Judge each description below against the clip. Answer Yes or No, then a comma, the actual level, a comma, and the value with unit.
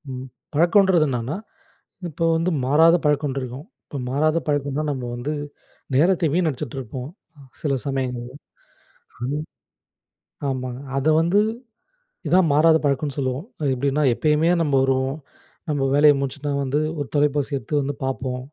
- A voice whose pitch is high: No, medium, 145 Hz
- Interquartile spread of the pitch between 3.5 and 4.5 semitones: No, average, 2.7 semitones